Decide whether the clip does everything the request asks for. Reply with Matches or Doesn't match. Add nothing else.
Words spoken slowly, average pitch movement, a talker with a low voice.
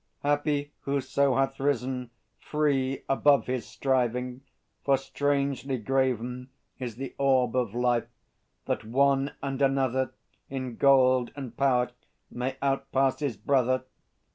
Doesn't match